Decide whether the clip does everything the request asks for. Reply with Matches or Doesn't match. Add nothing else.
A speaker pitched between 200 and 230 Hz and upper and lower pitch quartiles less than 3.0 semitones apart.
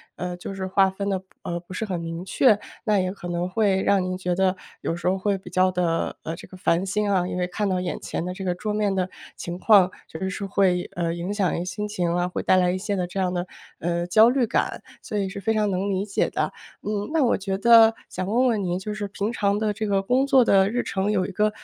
Doesn't match